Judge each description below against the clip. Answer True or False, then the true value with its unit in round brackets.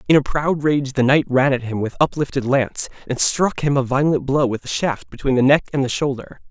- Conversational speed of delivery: False (250 wpm)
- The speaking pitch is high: False (135 Hz)